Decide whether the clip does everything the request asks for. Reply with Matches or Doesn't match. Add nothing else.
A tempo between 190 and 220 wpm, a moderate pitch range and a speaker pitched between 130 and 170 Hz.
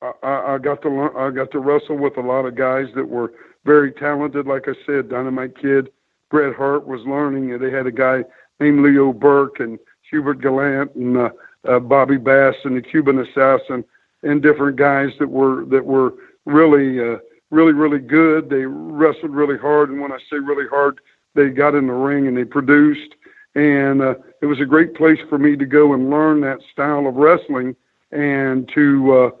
Doesn't match